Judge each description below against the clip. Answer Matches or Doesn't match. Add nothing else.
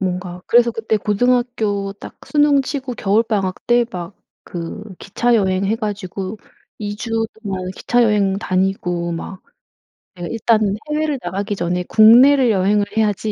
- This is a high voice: Matches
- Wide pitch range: Doesn't match